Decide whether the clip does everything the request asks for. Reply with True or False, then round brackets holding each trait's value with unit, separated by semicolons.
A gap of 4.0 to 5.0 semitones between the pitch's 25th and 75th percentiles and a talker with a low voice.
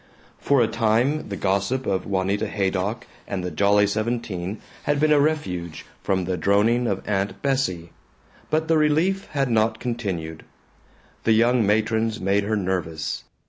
True (4.4 semitones; 105 Hz)